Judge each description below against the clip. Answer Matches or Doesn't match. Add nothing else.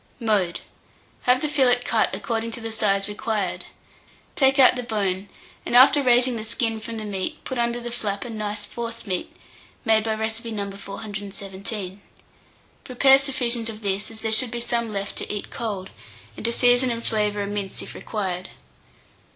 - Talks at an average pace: Matches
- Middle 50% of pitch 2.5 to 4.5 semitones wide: Matches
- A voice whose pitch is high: Matches